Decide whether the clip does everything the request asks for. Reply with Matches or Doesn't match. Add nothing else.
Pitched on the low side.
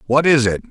Matches